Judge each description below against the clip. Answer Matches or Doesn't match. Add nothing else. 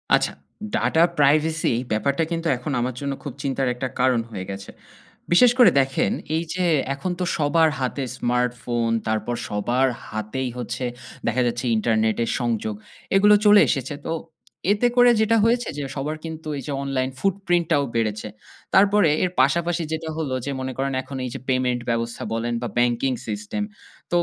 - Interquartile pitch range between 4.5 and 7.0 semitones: Matches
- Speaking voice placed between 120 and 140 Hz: Matches